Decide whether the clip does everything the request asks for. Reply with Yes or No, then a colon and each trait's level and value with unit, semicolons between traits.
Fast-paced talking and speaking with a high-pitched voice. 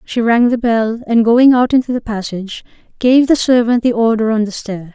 Yes: fast, 220 wpm; high, 230 Hz